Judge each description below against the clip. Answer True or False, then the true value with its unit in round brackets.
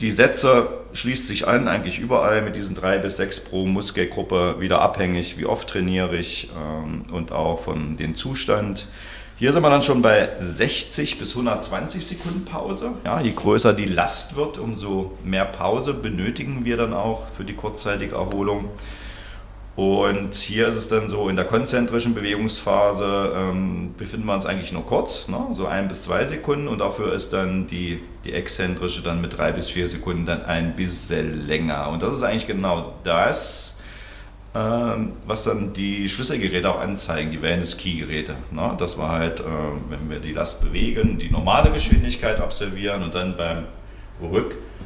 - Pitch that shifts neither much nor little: True (3.4 semitones)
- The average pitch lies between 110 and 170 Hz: False (95 Hz)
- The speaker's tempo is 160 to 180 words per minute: True (170 wpm)